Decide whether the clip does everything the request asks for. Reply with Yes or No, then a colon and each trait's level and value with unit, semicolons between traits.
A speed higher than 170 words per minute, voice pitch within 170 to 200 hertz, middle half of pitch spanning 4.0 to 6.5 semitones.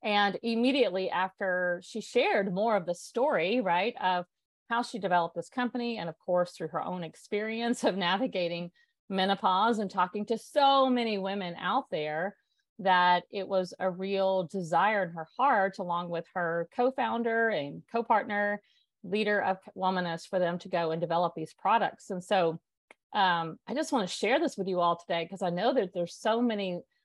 Yes: average, 180 wpm; high, 190 Hz; average, 4.3 semitones